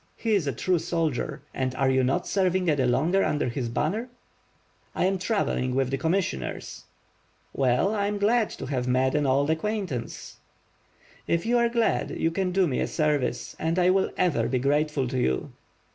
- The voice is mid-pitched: Yes, medium, 155 Hz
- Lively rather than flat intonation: Yes, wide, 6.6 semitones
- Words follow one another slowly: No, average, 180 wpm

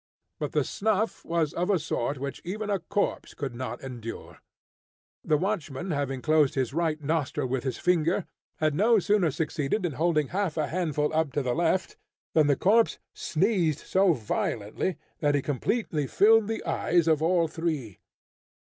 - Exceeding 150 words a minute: Yes, average, 165 wpm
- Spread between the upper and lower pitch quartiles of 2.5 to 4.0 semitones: No, average, 4.5 semitones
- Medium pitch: Yes, medium, 160 Hz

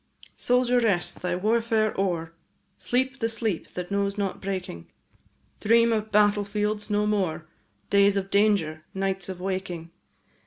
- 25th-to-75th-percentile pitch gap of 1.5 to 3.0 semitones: Yes, narrow, 2.6 semitones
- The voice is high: Yes, high, 200 Hz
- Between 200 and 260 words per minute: No, average, 140 wpm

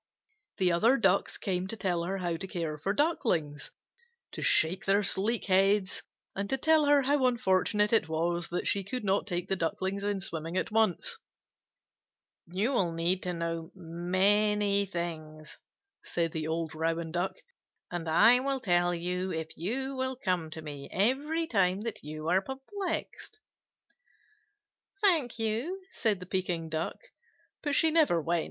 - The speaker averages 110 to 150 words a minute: No, average, 160 wpm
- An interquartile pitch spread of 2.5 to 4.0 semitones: No, average, 5.0 semitones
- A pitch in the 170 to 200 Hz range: Yes, high, 190 Hz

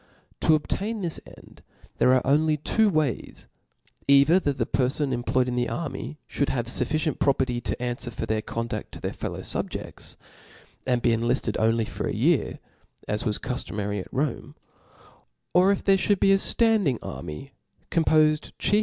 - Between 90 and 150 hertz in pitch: Yes, low, 135 Hz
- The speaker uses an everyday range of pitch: Yes, average, 4.7 semitones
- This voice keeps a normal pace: Yes, average, 170 wpm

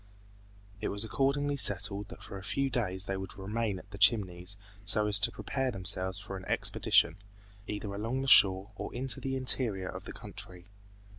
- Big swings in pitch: No, average, 4.1 semitones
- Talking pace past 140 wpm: Yes, average, 180 wpm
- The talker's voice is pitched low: Yes, low, 100 Hz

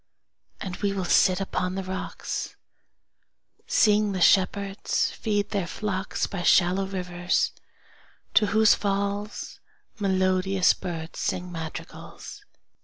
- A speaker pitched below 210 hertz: Yes, high, 190 Hz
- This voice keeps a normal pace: No, slow, 110 wpm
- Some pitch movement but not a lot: No, narrow, 1.8 semitones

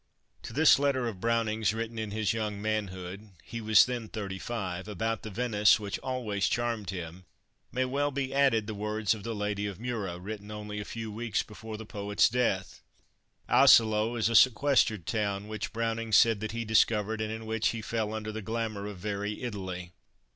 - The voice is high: No, low, 110 Hz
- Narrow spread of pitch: Yes, narrow, 1.9 semitones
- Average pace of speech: Yes, average, 190 wpm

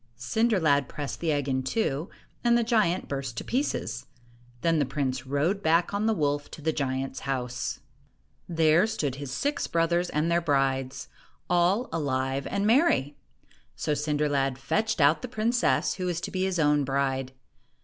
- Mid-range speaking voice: Yes, medium, 150 Hz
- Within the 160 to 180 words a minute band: Yes, average, 170 wpm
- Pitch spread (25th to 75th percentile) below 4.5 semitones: No, wide, 5.4 semitones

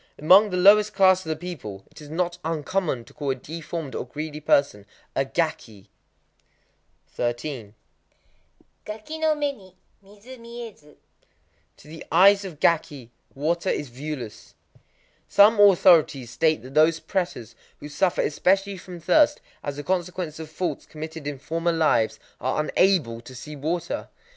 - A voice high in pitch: No, medium, 160 Hz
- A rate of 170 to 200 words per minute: No, average, 145 wpm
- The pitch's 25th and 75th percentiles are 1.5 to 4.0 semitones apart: No, average, 4.6 semitones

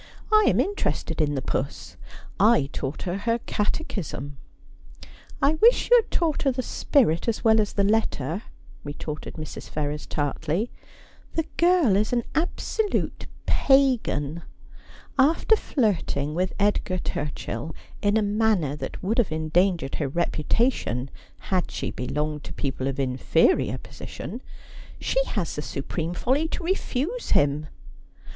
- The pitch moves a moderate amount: No, wide, 9.0 semitones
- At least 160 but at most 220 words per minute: No, average, 150 wpm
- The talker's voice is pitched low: No, high, 190 Hz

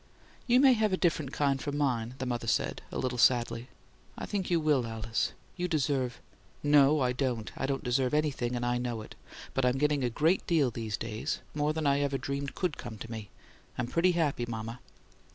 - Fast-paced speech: Yes, fast, 215 wpm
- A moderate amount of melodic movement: Yes, average, 3.7 semitones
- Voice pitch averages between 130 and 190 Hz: Yes, low, 135 Hz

